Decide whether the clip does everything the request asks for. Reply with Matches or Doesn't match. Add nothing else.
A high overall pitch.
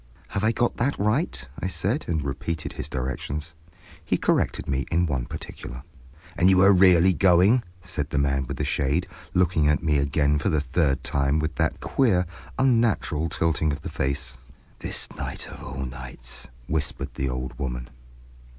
Doesn't match